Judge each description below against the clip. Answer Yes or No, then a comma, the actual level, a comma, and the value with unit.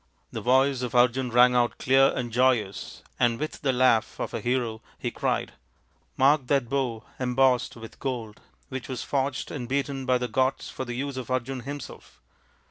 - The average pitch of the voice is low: Yes, low, 130 Hz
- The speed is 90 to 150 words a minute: No, average, 185 wpm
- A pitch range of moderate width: No, narrow, 1.7 semitones